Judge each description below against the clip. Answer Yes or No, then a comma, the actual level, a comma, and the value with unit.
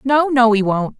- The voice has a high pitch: Yes, high, 240 Hz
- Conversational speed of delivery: No, fast, 240 wpm